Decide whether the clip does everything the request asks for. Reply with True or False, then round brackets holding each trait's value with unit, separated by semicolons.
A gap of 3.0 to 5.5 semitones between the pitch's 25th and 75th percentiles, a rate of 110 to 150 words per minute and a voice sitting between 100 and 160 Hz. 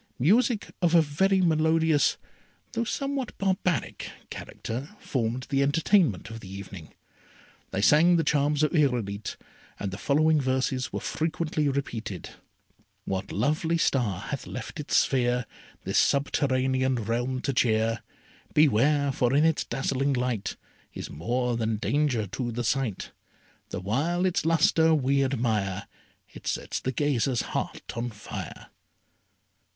True (5.1 semitones; 135 wpm; 135 Hz)